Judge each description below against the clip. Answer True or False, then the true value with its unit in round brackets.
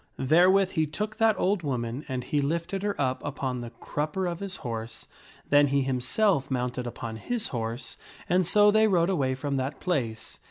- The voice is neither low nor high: True (145 Hz)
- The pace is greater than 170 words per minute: True (190 wpm)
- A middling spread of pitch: False (6.6 semitones)